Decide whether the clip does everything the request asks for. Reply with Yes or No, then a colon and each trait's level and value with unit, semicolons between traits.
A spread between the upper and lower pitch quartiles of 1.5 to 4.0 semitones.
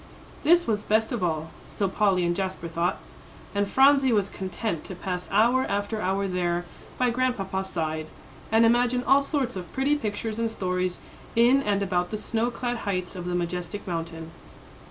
No: average, 4.7 semitones